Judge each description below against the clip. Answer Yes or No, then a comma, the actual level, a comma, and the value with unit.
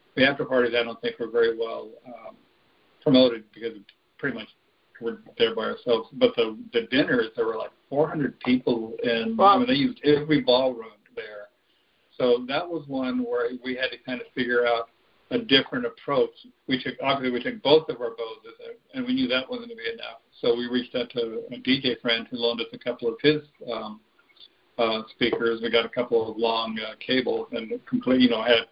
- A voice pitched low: Yes, low, 130 Hz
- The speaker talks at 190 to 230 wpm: Yes, fast, 205 wpm